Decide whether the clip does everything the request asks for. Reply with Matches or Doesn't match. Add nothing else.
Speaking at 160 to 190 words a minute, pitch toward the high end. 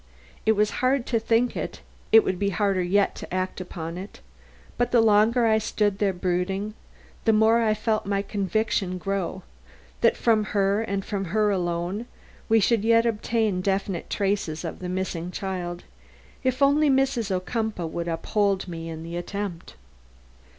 Matches